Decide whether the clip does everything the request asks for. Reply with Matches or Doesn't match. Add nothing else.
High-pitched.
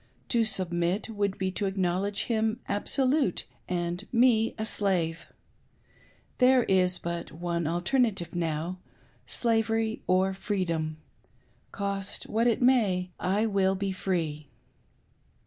Matches